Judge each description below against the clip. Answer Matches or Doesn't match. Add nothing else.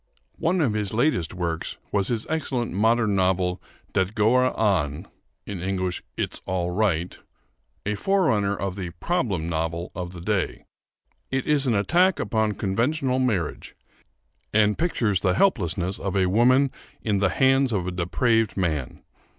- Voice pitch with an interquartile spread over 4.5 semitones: Matches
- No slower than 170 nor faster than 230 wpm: Doesn't match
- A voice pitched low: Matches